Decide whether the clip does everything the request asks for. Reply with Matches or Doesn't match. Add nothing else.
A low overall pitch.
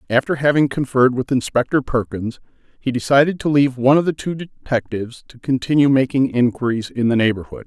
Matches